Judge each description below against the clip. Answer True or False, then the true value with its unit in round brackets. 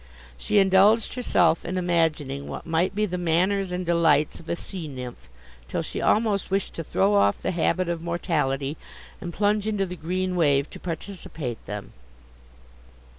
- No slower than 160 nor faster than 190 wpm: True (165 wpm)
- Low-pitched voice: False (175 Hz)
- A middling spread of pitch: True (3.9 semitones)